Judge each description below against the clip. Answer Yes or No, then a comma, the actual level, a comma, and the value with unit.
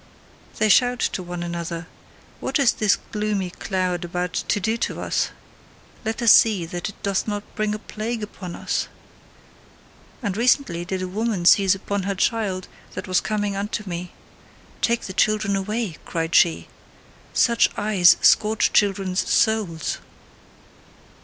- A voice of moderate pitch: No, high, 200 Hz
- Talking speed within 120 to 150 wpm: Yes, average, 145 wpm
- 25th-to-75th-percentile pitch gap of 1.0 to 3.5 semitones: Yes, average, 3.1 semitones